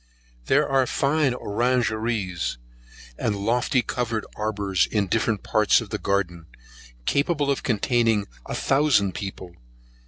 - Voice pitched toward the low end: Yes, low, 110 Hz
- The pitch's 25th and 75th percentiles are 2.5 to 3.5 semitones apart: No, average, 4.3 semitones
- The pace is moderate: No, slow, 120 wpm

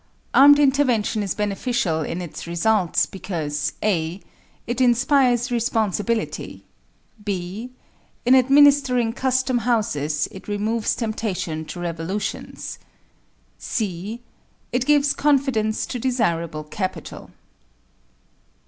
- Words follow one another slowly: Yes, slow, 95 wpm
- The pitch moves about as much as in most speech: No, wide, 5.9 semitones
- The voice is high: Yes, high, 220 Hz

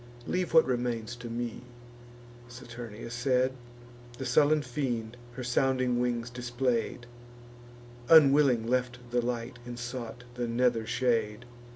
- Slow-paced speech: Yes, slow, 115 wpm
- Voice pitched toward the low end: Yes, low, 120 Hz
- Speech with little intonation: Yes, narrow, 1.4 semitones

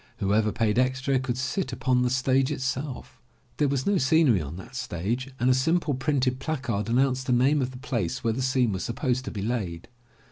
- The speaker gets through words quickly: Yes, fast, 210 wpm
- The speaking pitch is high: No, low, 130 Hz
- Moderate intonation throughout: No, narrow, 2.3 semitones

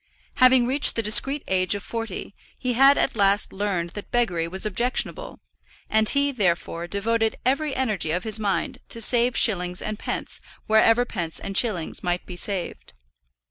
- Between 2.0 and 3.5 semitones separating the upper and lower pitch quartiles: No, average, 4.7 semitones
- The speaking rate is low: No, average, 165 wpm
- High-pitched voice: Yes, high, 215 Hz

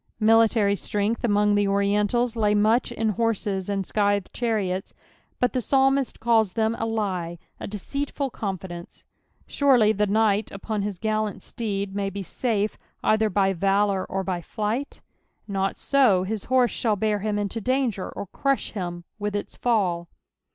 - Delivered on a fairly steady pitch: Yes, narrow, 2.3 semitones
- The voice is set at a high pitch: Yes, high, 210 Hz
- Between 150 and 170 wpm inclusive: Yes, average, 155 wpm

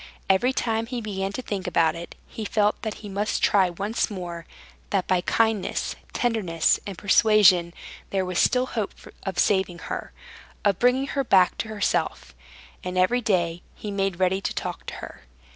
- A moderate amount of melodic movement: Yes, average, 3.4 semitones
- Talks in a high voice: Yes, high, 200 Hz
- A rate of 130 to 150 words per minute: No, average, 175 wpm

